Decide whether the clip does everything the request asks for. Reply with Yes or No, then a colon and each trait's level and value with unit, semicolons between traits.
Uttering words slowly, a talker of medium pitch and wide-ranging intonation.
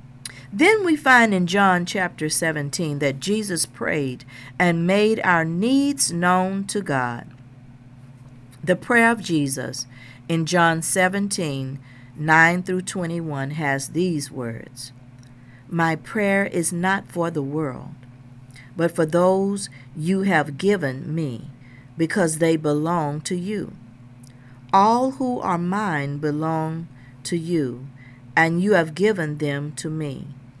Yes: slow, 120 wpm; medium, 160 Hz; wide, 6.1 semitones